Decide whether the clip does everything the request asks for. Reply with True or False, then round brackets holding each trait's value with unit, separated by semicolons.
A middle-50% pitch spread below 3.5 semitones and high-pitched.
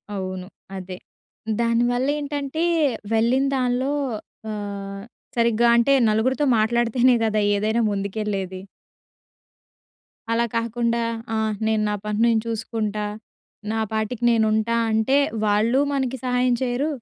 True (2.8 semitones; 230 Hz)